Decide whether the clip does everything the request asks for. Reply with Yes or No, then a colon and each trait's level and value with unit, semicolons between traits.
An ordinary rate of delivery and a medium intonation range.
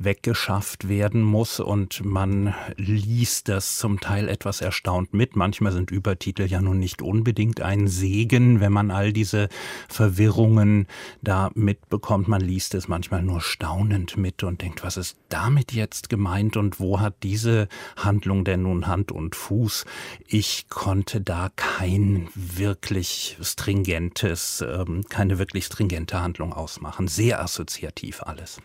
No: average, 140 wpm; narrow, 2.1 semitones